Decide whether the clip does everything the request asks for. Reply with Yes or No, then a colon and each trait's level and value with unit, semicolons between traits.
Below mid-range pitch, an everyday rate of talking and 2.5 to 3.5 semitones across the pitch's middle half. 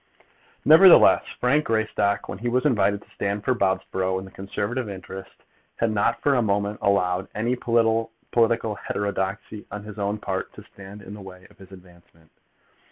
Yes: low, 100 Hz; average, 165 wpm; average, 2.9 semitones